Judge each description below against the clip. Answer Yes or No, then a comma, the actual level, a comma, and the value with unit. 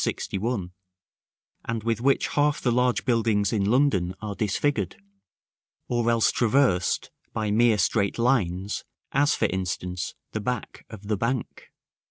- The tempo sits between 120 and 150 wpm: Yes, slow, 135 wpm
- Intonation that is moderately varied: Yes, average, 3.7 semitones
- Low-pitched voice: Yes, low, 110 Hz